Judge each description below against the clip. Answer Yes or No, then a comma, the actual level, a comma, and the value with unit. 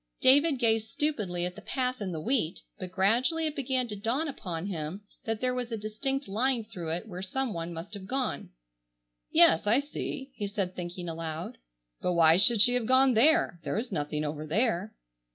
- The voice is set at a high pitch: Yes, high, 215 Hz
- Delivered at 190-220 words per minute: Yes, average, 195 wpm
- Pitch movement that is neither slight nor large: No, wide, 6.4 semitones